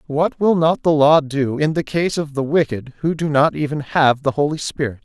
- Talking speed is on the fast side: Yes, fast, 240 wpm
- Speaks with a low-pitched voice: No, medium, 150 Hz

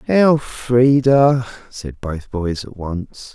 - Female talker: No, male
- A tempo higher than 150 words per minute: No, slow, 110 wpm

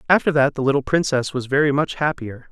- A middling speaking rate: No, fast, 215 wpm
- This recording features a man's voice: Yes, male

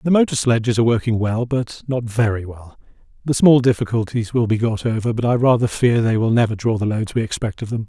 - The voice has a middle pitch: No, low, 115 Hz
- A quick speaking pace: Yes, fast, 235 wpm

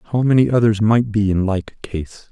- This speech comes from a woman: No, male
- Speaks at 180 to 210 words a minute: Yes, fast, 205 wpm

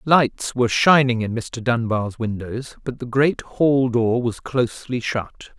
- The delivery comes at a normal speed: Yes, average, 160 wpm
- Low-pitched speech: Yes, low, 120 Hz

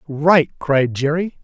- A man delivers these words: Yes, male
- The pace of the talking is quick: No, slow, 125 wpm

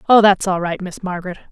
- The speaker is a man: No, female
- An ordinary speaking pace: No, fast, 235 wpm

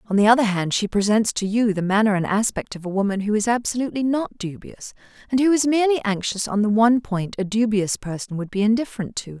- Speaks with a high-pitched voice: Yes, high, 215 Hz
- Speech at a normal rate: No, fast, 230 wpm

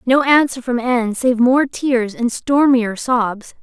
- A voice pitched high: Yes, high, 245 Hz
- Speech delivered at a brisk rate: No, average, 165 wpm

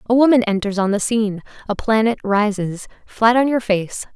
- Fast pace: No, average, 190 wpm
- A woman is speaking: Yes, female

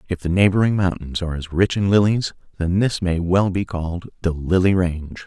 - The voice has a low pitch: Yes, very low, 90 Hz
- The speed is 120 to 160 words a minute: No, fast, 205 wpm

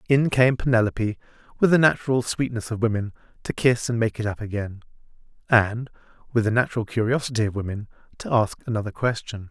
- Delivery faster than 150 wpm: No, average, 145 wpm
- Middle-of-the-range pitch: No, low, 115 Hz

